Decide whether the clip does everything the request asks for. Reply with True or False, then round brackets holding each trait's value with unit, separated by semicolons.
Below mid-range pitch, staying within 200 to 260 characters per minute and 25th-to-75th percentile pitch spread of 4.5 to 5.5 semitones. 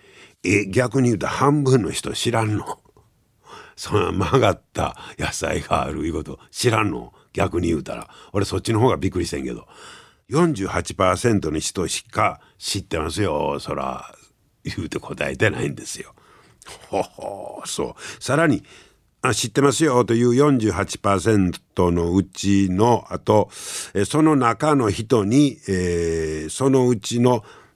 True (110 Hz; 255 characters per minute; 5.2 semitones)